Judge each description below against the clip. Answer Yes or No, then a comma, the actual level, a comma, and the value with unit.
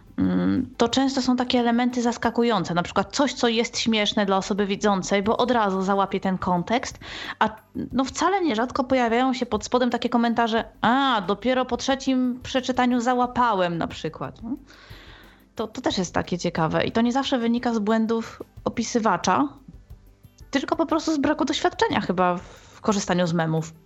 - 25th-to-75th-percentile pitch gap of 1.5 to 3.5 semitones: No, average, 4.6 semitones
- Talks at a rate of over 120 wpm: Yes, fast, 160 wpm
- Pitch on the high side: Yes, high, 235 Hz